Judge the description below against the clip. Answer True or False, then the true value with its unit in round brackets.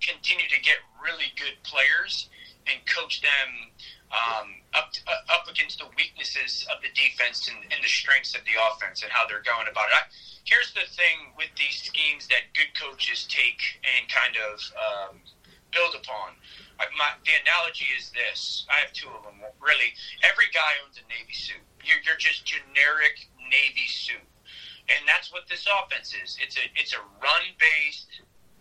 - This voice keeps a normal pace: True (180 wpm)